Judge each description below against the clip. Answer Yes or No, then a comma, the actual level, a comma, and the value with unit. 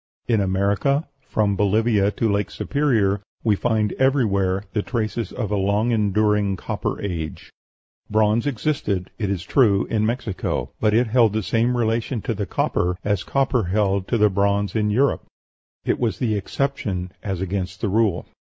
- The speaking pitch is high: No, low, 105 Hz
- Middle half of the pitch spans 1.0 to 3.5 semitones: Yes, average, 2.8 semitones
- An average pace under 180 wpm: Yes, average, 165 wpm